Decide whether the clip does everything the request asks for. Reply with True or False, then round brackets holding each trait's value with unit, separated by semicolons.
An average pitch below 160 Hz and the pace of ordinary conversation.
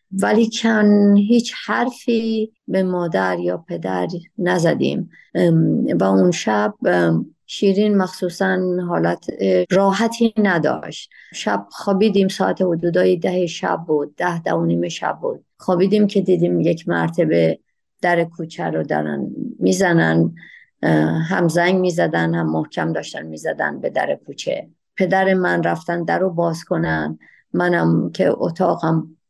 False (175 Hz; 115 wpm)